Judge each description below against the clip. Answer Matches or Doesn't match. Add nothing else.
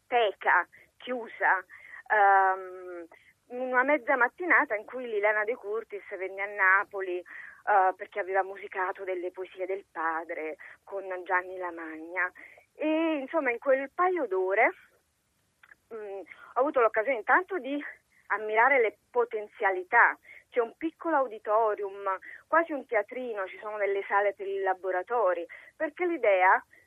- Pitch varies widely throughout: Matches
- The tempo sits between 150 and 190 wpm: Doesn't match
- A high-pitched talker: Matches